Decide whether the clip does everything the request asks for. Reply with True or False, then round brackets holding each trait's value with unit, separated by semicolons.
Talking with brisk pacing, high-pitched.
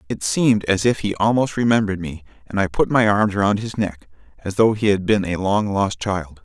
False (235 wpm; 100 Hz)